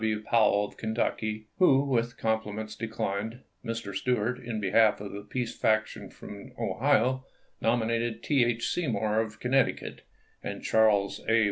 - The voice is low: Yes, low, 110 Hz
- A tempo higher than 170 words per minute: No, average, 140 wpm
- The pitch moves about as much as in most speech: No, narrow, 2.0 semitones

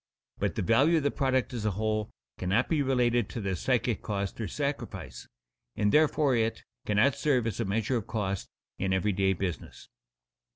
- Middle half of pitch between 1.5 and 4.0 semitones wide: No, average, 4.8 semitones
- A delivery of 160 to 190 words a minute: Yes, average, 180 wpm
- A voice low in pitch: Yes, low, 115 Hz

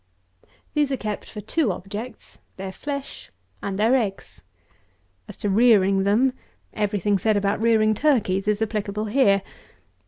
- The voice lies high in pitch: Yes, high, 210 Hz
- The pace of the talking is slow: No, average, 145 wpm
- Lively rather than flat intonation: No, average, 2.9 semitones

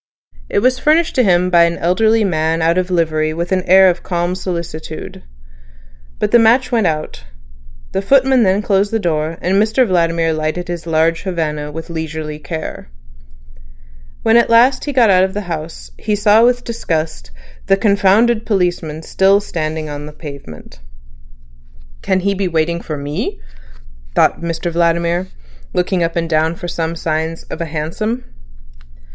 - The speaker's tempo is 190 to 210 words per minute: No, average, 165 wpm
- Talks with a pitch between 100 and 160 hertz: No, medium, 175 Hz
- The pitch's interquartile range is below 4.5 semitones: Yes, average, 4.0 semitones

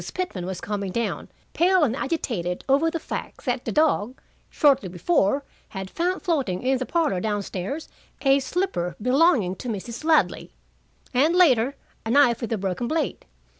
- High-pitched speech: Yes, very high, 255 Hz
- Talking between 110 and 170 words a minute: Yes, average, 165 wpm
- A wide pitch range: Yes, wide, 7.7 semitones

